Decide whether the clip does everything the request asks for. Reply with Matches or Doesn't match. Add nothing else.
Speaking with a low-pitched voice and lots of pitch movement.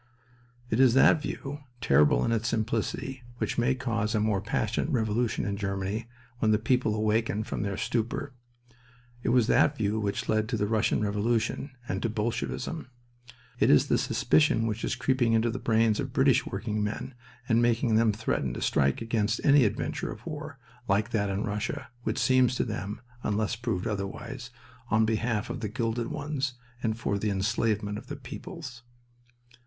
Doesn't match